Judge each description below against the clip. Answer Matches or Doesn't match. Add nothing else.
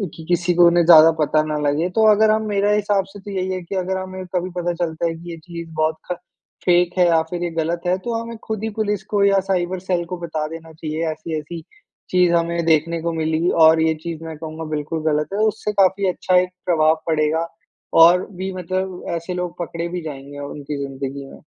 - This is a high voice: Doesn't match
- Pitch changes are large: Doesn't match